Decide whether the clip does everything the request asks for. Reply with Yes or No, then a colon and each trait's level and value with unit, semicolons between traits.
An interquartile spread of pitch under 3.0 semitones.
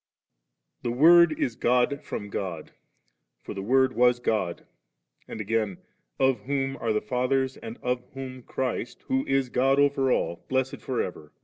No: average, 3.3 semitones